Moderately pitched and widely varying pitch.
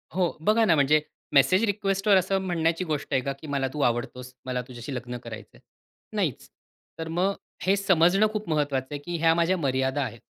Yes: medium, 160 Hz; wide, 6.0 semitones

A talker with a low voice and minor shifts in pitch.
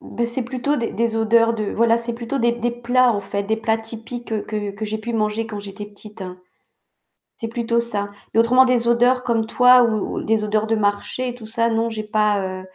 No: high, 225 Hz; narrow, 1.8 semitones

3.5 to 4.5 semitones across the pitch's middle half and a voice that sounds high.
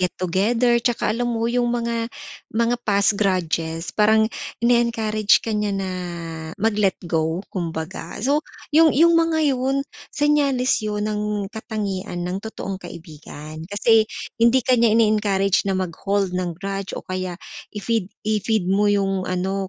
Yes: average, 3.8 semitones; high, 210 Hz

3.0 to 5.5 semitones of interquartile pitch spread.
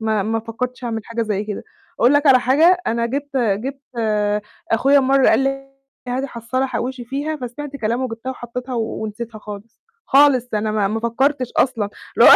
Yes: average, 3.3 semitones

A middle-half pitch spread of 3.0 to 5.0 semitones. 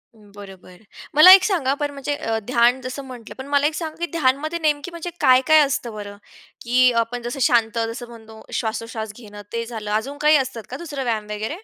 Yes: average, 4.5 semitones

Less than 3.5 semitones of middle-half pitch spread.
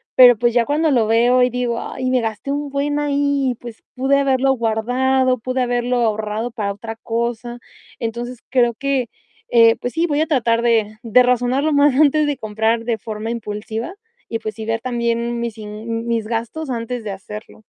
Yes: narrow, 2.5 semitones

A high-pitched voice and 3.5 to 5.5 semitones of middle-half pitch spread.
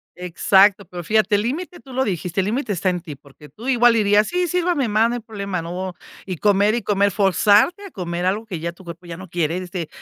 Yes: high, 200 Hz; average, 4.1 semitones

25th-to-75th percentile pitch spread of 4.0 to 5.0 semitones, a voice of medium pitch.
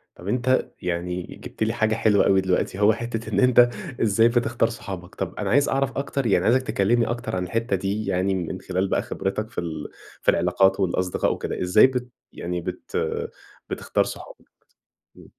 No: average, 4.3 semitones; low, 100 Hz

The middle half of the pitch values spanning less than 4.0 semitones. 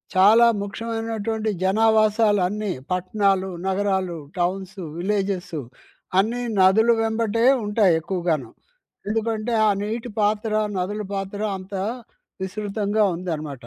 Yes: average, 2.8 semitones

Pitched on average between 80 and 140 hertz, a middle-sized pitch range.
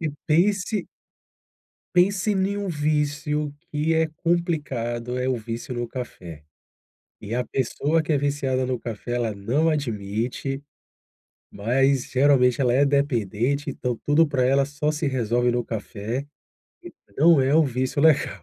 Yes: low, 135 Hz; average, 3.8 semitones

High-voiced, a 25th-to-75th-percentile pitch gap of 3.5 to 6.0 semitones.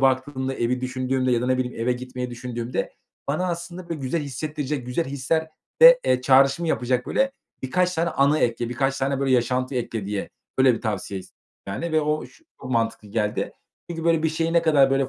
No: low, 130 Hz; average, 3.9 semitones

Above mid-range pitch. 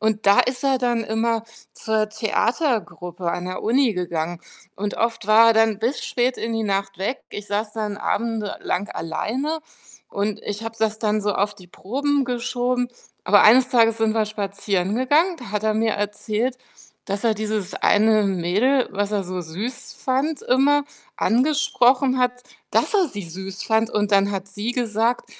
Yes: high, 220 Hz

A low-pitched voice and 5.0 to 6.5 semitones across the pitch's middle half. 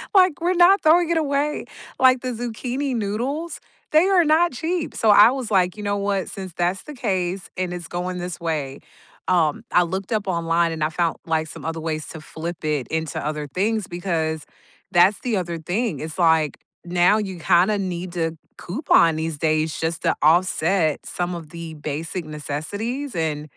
No: medium, 180 Hz; wide, 5.6 semitones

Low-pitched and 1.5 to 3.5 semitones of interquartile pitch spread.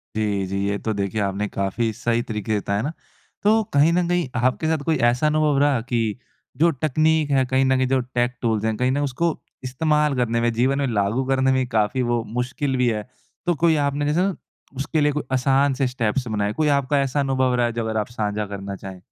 No: low, 130 Hz; average, 4.4 semitones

